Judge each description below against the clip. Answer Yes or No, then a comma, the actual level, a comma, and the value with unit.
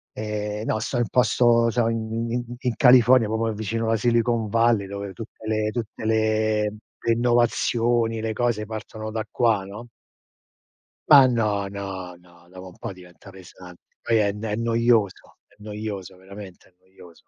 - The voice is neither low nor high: No, low, 110 Hz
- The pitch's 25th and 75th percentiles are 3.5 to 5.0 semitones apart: No, narrow, 2.6 semitones